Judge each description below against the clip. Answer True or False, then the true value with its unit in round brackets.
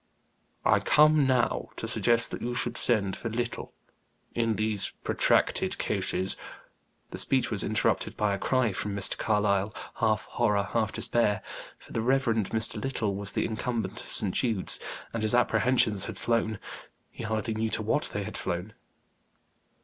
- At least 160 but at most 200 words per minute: True (165 wpm)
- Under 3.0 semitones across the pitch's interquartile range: True (2.5 semitones)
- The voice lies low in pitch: True (110 Hz)